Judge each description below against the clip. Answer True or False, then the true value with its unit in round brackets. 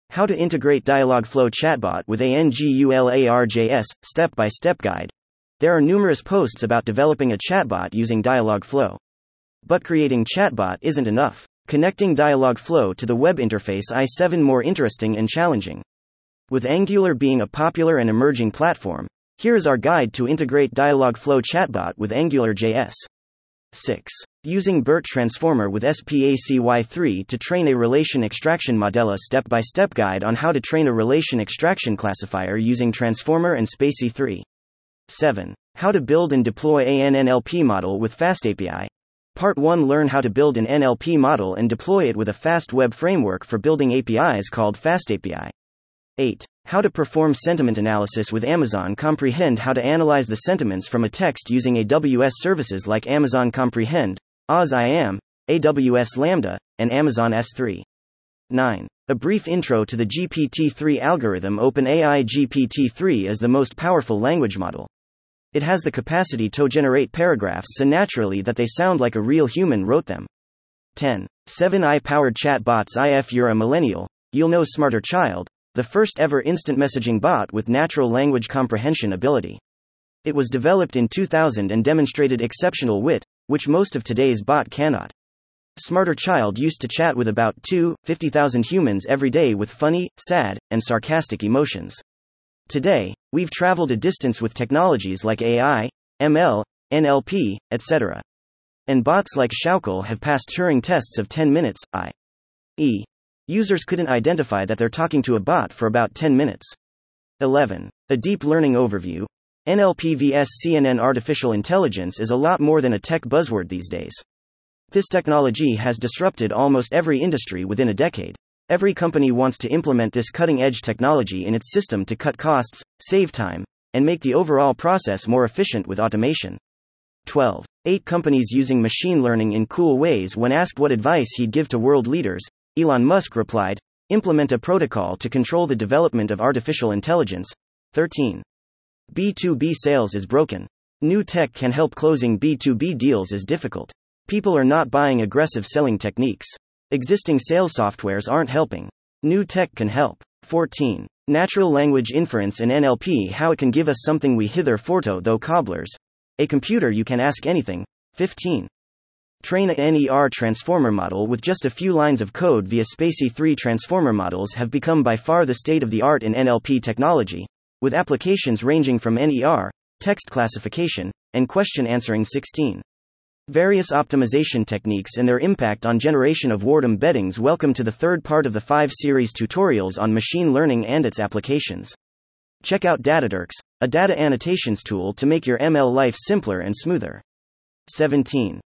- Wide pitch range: True (6.0 semitones)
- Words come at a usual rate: True (155 wpm)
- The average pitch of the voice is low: True (130 Hz)